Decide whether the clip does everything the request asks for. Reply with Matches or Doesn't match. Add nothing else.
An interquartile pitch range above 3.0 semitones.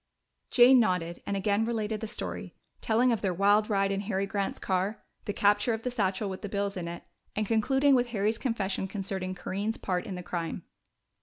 Doesn't match